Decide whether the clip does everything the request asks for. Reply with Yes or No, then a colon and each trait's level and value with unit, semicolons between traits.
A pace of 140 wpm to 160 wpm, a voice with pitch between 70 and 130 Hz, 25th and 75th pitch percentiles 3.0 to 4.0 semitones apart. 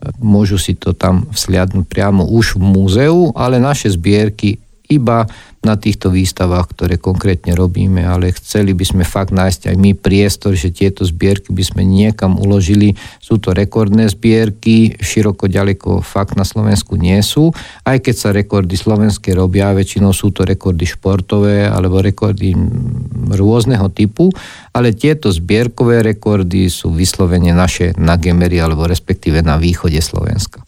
No: average, 150 wpm; low, 100 Hz; narrow, 2.5 semitones